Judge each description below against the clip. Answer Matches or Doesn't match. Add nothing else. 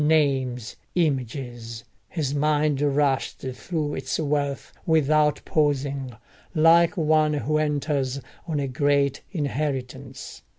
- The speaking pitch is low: Doesn't match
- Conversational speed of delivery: Doesn't match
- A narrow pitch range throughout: Matches